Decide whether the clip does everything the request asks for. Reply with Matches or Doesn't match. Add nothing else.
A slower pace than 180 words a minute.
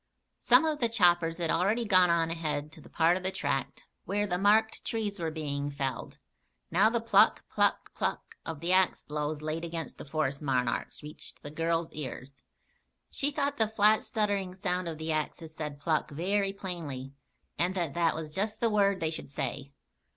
Doesn't match